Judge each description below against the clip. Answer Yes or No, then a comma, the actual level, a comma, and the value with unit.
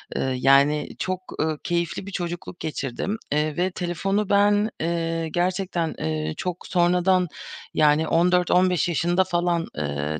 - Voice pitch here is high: No, medium, 175 Hz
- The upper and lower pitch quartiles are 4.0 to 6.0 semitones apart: No, average, 3.0 semitones